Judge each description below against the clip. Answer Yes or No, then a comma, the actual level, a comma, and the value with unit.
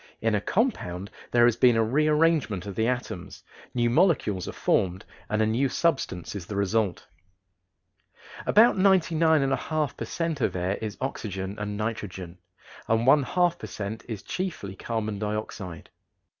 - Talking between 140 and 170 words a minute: Yes, average, 155 wpm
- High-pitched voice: No, low, 110 Hz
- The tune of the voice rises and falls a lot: Yes, wide, 6.9 semitones